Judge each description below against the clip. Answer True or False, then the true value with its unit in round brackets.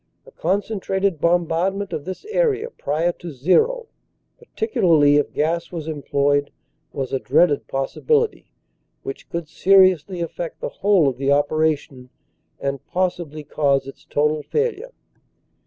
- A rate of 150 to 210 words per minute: False (135 wpm)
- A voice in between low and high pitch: True (170 Hz)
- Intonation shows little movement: False (5.2 semitones)